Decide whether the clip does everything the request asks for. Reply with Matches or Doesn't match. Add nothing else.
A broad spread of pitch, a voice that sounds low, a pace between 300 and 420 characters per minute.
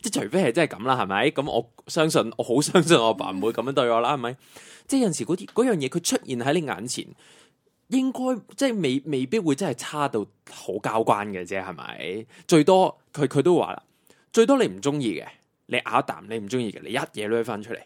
Doesn't match